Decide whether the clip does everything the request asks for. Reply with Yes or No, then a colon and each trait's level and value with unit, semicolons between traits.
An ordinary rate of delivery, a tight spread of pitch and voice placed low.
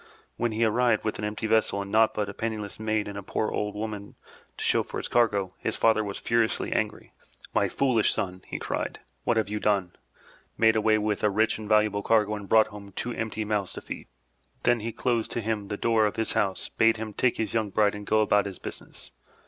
No: fast, 230 wpm; narrow, 1.5 semitones; low, 110 Hz